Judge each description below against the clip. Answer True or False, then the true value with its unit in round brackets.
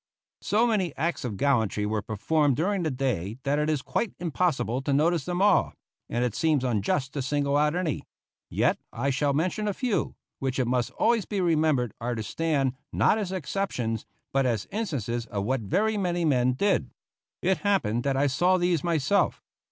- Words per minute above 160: True (185 wpm)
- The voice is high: False (145 Hz)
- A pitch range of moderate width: False (6.3 semitones)